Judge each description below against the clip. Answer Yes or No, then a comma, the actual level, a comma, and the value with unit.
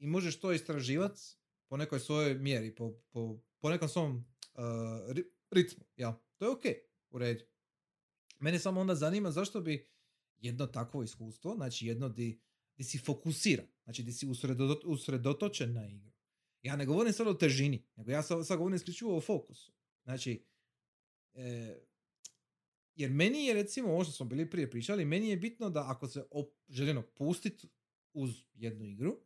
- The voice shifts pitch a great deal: Yes, wide, 6.4 semitones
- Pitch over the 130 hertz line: Yes, medium, 140 Hz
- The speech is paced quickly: Yes, fast, 165 wpm